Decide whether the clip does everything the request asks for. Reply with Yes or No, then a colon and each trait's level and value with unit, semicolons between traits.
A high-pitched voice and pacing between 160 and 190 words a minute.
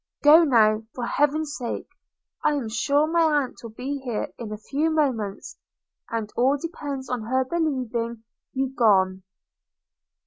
No: very high, 260 Hz; average, 150 wpm